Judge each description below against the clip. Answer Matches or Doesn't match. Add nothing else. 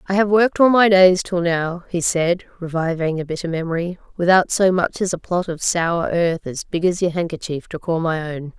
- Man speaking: Doesn't match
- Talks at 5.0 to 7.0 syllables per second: Matches